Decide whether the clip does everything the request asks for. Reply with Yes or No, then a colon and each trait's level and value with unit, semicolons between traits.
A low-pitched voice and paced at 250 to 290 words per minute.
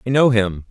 Yes: low, 115 Hz; fast, 255 wpm